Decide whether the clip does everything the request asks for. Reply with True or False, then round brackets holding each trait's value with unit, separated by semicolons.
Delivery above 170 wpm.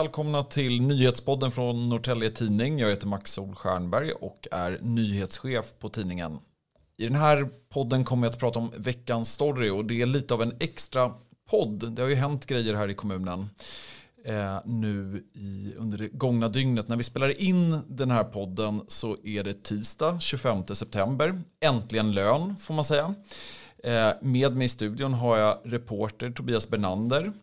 False (165 wpm)